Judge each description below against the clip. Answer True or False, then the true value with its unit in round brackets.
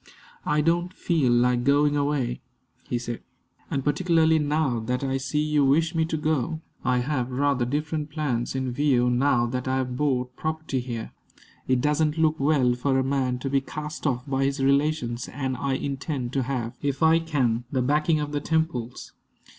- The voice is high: False (140 Hz)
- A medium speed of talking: True (185 wpm)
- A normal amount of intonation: True (3.2 semitones)